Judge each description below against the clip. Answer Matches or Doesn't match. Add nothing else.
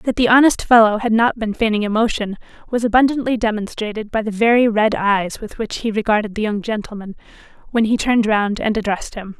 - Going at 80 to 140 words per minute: Doesn't match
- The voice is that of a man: Doesn't match